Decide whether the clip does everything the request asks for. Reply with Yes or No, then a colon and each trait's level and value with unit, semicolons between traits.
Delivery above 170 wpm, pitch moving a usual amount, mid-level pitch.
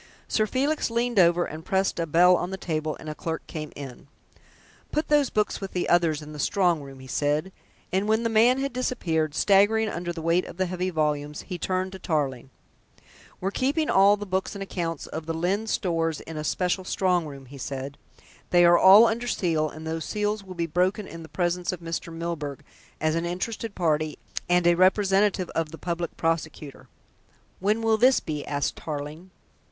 Yes: average, 195 wpm; average, 3.8 semitones; medium, 175 Hz